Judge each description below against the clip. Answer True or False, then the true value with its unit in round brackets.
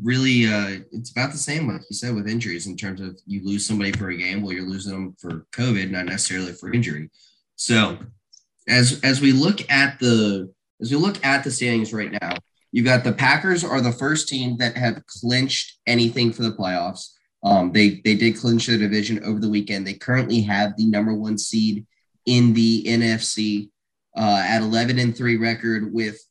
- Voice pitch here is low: True (115 Hz)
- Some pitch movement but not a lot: True (3.0 semitones)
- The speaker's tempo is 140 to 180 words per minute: False (200 wpm)